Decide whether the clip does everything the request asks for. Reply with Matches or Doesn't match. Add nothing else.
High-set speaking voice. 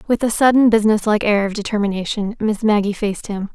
Matches